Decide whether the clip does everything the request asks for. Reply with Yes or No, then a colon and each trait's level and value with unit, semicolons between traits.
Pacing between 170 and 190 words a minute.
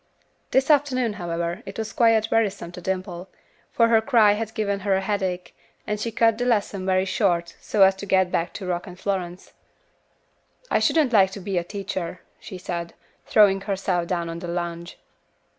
Yes: average, 185 wpm